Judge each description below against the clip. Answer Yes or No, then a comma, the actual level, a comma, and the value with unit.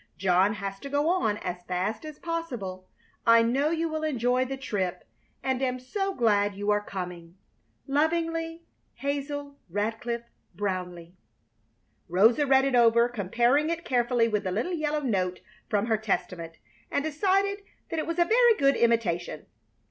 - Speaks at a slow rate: No, average, 155 wpm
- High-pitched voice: Yes, high, 240 Hz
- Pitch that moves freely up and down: Yes, wide, 6.9 semitones